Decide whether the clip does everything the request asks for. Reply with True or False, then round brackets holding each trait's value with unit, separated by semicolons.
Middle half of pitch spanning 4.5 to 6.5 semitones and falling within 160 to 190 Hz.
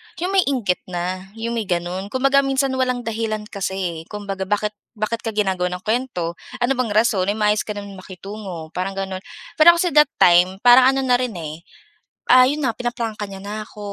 False (4.9 semitones; 210 Hz)